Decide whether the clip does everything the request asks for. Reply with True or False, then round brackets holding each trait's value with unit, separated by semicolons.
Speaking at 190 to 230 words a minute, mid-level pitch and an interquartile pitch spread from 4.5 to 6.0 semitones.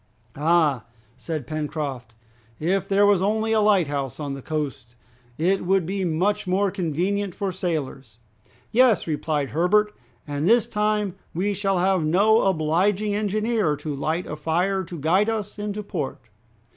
False (145 wpm; 180 Hz; 4.9 semitones)